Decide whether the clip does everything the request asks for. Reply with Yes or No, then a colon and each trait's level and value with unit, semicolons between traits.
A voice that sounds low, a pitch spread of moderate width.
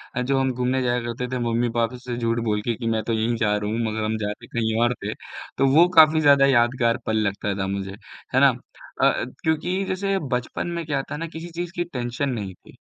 Yes: low, 120 Hz; average, 3.9 semitones